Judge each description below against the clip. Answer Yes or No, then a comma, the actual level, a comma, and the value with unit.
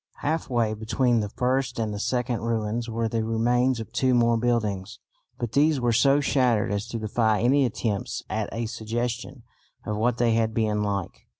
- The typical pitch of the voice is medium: No, low, 115 Hz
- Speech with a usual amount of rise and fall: No, narrow, 2.1 semitones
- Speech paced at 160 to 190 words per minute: Yes, average, 185 wpm